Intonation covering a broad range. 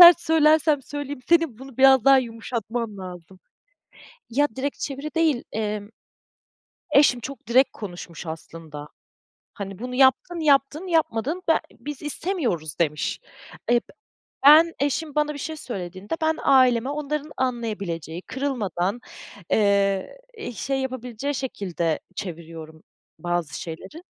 Yes: wide, 7.1 semitones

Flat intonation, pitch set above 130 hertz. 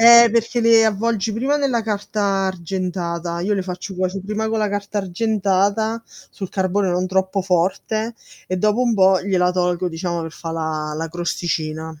No: average, 3.6 semitones; high, 190 Hz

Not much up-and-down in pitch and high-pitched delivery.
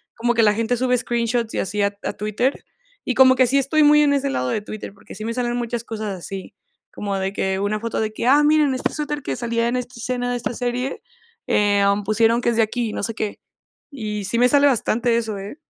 No: average, 3.1 semitones; high, 235 Hz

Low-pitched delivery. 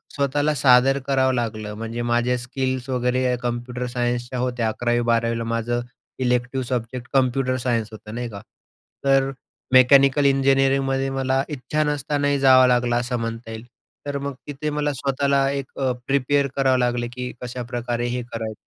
Yes: low, 125 Hz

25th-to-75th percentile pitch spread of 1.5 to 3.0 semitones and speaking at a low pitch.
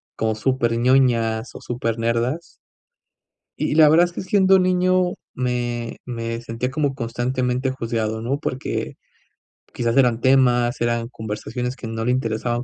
Yes: narrow, 2.4 semitones; low, 125 Hz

